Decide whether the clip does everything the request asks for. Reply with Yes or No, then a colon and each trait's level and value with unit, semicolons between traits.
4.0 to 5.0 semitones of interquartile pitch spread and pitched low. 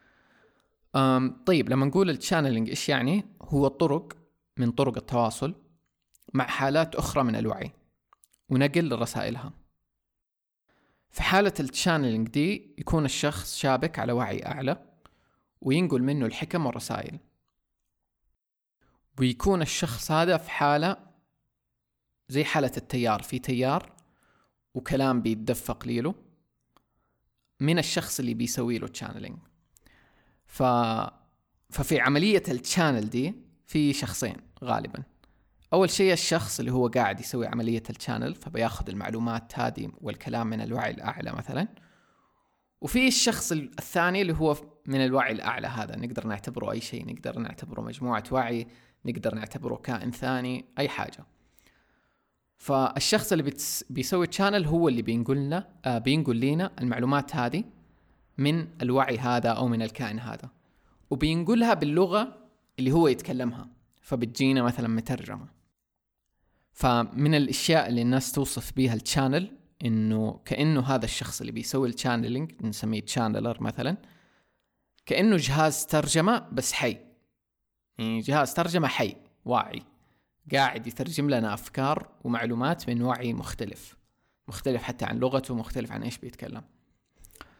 Yes: average, 4.4 semitones; low, 130 Hz